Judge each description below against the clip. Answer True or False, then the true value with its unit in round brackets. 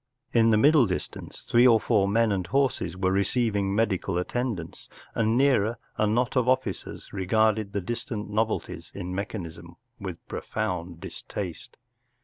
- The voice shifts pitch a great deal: False (3.5 semitones)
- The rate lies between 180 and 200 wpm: False (165 wpm)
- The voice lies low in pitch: True (105 Hz)